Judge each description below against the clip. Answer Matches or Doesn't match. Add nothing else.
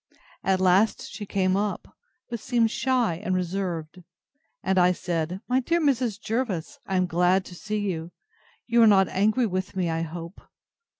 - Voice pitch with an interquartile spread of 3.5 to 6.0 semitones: Matches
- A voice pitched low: Doesn't match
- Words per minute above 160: Matches